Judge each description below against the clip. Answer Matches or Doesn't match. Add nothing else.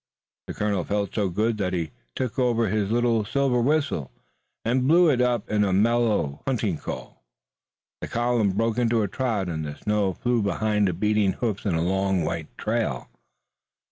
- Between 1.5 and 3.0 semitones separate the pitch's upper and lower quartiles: Doesn't match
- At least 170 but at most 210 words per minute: Matches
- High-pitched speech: Doesn't match